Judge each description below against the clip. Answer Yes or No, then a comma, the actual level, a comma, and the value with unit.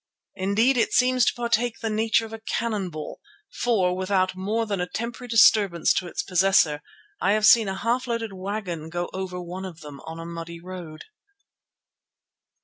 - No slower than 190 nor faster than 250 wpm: No, average, 175 wpm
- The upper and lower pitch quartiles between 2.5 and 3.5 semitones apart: No, average, 4.3 semitones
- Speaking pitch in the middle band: No, high, 195 Hz